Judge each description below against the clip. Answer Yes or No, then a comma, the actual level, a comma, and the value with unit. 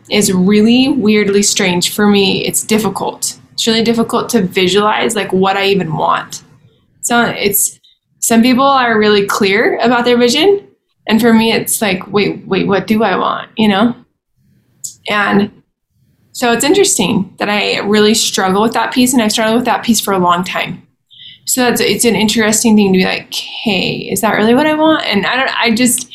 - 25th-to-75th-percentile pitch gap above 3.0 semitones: No, average, 2.7 semitones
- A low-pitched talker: No, high, 215 Hz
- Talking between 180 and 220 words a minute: Yes, average, 190 wpm